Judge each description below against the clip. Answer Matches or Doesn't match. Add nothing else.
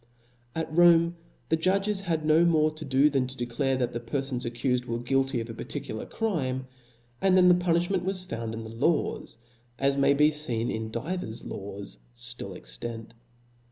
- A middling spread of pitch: Doesn't match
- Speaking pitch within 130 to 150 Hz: Matches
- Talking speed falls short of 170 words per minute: Doesn't match